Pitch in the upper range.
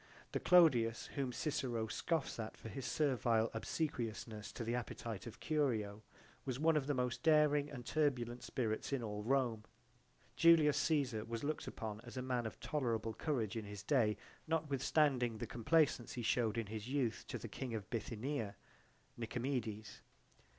No: low, 120 Hz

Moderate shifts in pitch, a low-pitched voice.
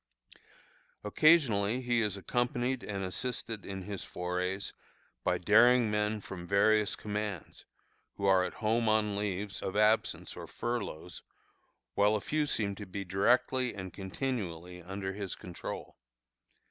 Yes: average, 3.1 semitones; low, 105 Hz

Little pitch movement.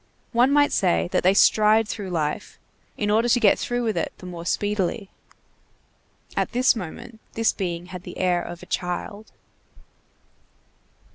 No: average, 4.1 semitones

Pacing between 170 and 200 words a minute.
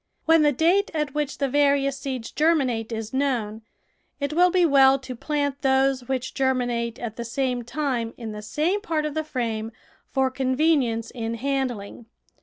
Yes: average, 175 wpm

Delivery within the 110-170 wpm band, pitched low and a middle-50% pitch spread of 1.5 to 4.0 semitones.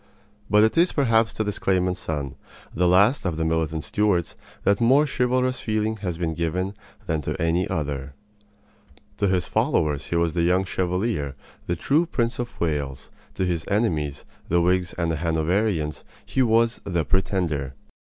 No: average, 165 wpm; very low, 90 Hz; average, 5.1 semitones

